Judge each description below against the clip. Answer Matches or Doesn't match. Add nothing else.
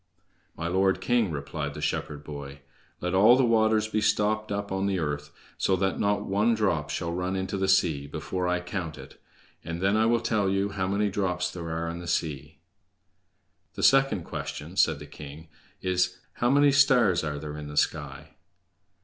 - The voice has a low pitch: Matches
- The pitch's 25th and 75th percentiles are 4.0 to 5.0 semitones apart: Matches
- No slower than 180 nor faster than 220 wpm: Matches